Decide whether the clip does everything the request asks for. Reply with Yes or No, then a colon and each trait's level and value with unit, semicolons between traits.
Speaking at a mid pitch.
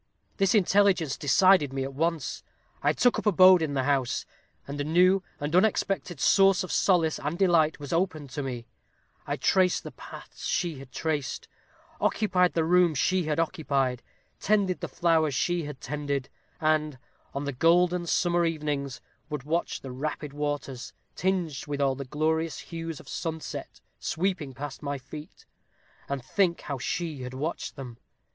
Yes: medium, 155 Hz